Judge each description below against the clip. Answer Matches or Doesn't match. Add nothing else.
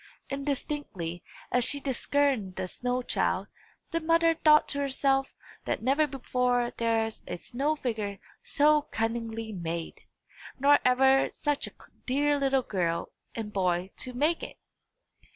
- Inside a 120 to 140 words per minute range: Matches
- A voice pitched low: Doesn't match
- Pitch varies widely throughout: Doesn't match